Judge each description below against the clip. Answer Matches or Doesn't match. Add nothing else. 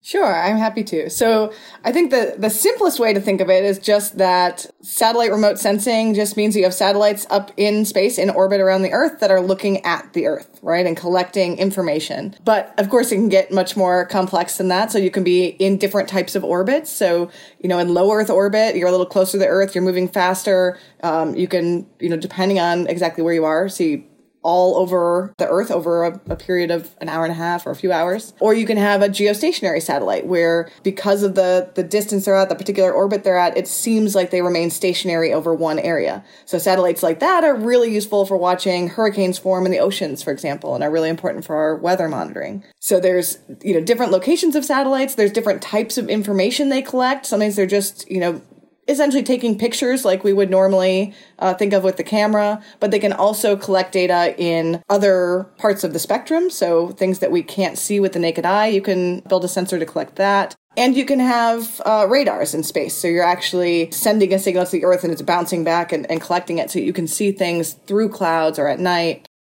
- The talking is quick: Matches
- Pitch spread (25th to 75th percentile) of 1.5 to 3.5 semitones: Matches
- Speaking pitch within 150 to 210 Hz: Matches